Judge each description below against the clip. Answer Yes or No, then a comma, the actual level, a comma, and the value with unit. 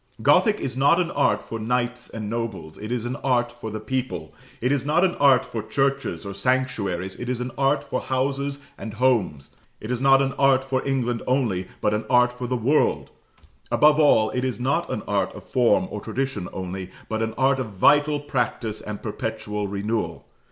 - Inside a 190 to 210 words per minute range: Yes, average, 200 wpm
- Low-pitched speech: Yes, low, 125 Hz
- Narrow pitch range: No, average, 3.8 semitones